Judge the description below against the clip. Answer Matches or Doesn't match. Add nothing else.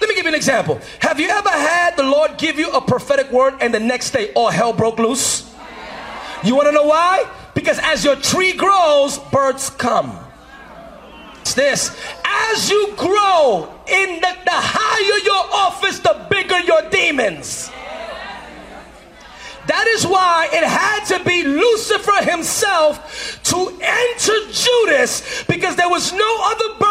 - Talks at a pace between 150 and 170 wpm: Matches